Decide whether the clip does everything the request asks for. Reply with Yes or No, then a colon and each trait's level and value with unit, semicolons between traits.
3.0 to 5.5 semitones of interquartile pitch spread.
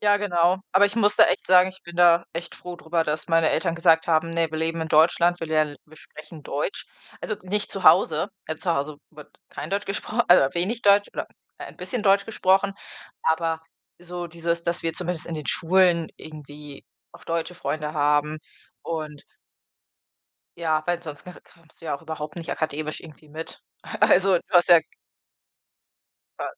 No: narrow, 2.4 semitones